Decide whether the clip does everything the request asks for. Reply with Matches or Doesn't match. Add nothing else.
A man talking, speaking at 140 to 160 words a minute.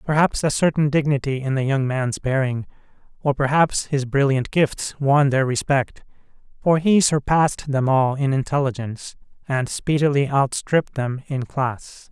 Matches